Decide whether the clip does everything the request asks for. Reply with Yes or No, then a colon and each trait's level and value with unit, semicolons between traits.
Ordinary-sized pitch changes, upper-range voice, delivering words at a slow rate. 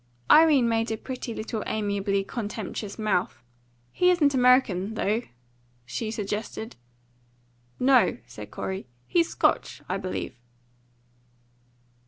Yes: average, 3.9 semitones; high, 220 Hz; slow, 105 wpm